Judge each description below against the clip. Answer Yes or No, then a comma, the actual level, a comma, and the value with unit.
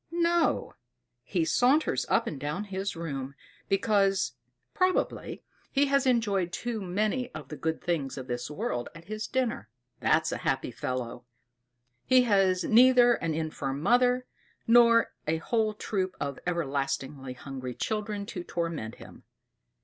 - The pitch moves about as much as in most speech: No, wide, 7.9 semitones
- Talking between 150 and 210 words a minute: No, average, 140 wpm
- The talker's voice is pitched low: No, high, 190 Hz